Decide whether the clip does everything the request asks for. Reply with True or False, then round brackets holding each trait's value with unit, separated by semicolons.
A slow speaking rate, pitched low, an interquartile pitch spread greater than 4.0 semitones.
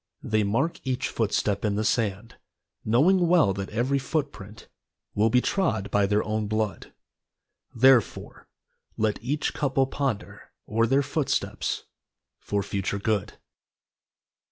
True (130 wpm; 110 Hz; 4.6 semitones)